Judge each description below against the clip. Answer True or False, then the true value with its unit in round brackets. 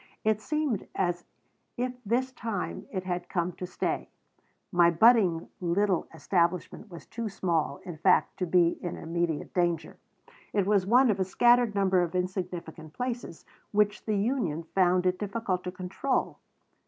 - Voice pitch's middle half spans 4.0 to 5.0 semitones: False (3.6 semitones)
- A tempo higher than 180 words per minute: False (155 wpm)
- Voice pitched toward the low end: False (185 Hz)